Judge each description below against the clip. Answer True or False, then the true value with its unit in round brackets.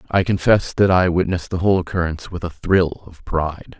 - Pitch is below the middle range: True (85 Hz)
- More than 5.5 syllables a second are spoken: True (6.0 syllables/s)